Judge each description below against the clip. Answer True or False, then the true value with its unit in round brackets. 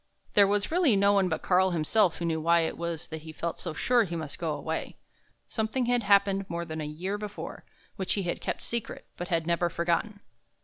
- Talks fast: True (220 wpm)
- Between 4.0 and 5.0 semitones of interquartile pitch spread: False (3.6 semitones)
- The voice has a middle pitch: True (180 Hz)